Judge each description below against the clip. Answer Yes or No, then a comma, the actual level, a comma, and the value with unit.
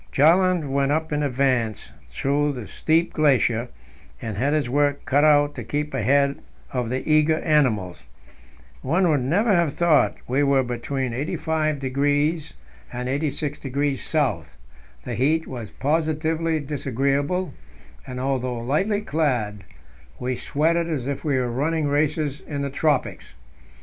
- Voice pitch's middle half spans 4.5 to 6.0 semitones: No, average, 3.2 semitones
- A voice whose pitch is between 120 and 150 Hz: Yes, medium, 140 Hz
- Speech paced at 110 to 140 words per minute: Yes, slow, 135 wpm